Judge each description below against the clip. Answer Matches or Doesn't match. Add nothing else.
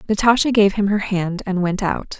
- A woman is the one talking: Matches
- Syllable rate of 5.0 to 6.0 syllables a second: Matches